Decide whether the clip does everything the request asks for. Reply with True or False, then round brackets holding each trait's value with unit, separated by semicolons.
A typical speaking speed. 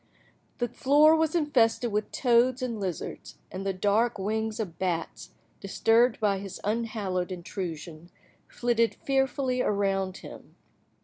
False (125 wpm)